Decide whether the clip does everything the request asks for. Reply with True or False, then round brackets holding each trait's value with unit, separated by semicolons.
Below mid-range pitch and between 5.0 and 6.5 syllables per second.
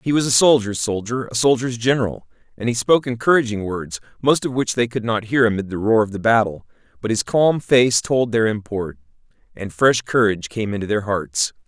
True (115 Hz; 5.5 syllables/s)